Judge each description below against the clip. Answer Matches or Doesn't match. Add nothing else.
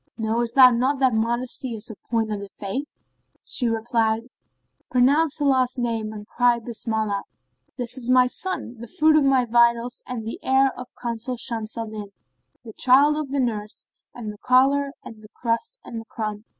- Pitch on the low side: Doesn't match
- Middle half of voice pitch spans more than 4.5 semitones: Doesn't match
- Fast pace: Doesn't match